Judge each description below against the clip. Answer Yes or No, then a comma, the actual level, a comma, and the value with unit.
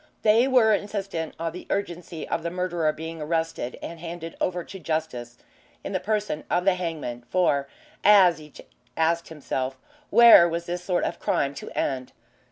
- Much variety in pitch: No, average, 2.8 semitones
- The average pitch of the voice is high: No, medium, 170 Hz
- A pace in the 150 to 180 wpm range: Yes, average, 170 wpm